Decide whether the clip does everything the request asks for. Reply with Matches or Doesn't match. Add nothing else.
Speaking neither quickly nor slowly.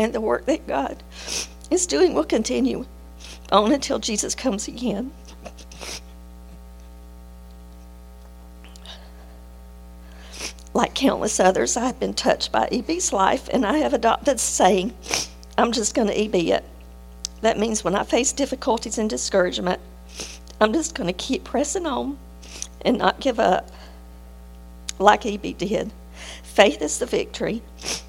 Doesn't match